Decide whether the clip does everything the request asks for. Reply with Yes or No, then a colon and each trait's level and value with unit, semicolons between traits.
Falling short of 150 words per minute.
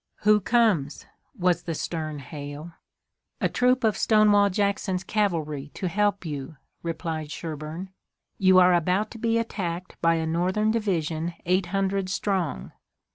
Yes: slow, 135 wpm